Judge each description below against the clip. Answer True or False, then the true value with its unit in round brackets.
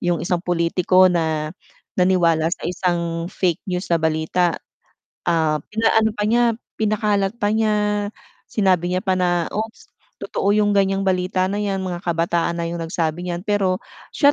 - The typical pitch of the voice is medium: True (180 Hz)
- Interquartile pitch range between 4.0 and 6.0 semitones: False (3.3 semitones)